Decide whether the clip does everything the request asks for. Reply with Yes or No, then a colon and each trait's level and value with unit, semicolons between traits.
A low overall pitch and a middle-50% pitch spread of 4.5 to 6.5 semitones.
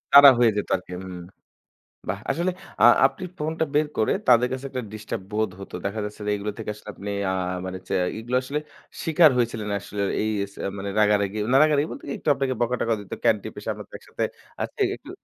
Yes: low, 115 Hz; average, 4.8 semitones